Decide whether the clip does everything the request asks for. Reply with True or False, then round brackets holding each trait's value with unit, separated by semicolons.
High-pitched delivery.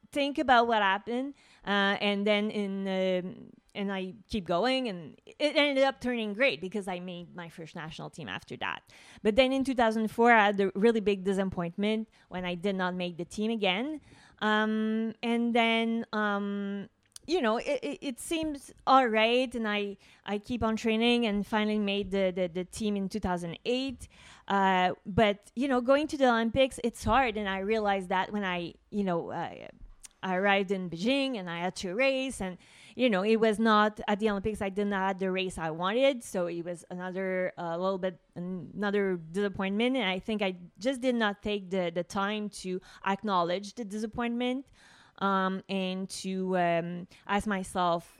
True (205 Hz)